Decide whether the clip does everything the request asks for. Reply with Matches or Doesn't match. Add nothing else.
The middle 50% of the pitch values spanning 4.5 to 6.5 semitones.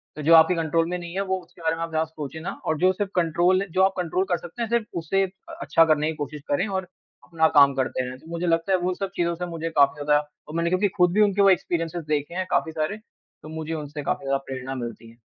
Doesn't match